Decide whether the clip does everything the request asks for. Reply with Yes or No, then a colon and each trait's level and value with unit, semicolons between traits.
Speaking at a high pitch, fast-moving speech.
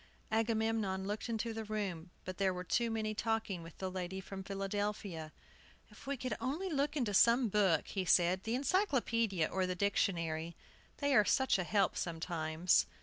No: high, 200 Hz; average, 170 wpm